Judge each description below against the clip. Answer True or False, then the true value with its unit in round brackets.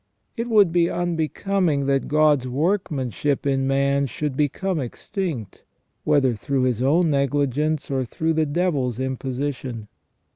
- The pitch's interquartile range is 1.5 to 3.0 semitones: False (3.6 semitones)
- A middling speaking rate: False (130 wpm)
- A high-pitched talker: False (140 Hz)